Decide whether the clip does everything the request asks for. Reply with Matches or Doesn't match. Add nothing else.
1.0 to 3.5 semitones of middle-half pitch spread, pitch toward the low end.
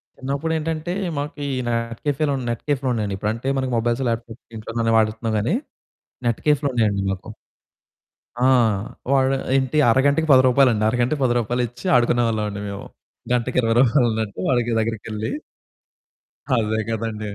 Matches